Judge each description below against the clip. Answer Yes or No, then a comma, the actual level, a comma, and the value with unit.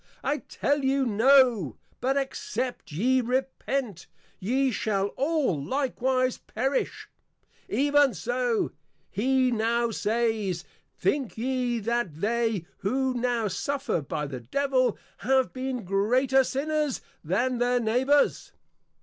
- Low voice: No, very high, 250 Hz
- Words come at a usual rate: No, slow, 110 wpm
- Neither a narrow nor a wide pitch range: Yes, average, 3.4 semitones